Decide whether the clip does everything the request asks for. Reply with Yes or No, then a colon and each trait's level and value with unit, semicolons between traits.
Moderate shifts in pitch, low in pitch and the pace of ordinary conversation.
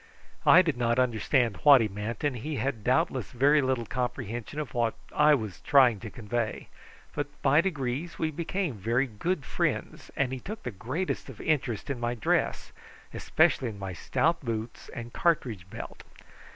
Yes: average, 4.3 semitones; low, 125 Hz; average, 165 wpm